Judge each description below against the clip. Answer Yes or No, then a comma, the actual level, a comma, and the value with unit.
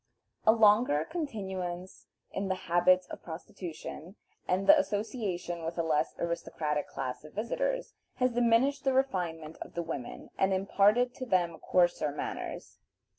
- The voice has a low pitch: No, medium, 185 Hz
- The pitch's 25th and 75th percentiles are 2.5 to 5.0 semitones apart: No, wide, 5.4 semitones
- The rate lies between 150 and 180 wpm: No, average, 140 wpm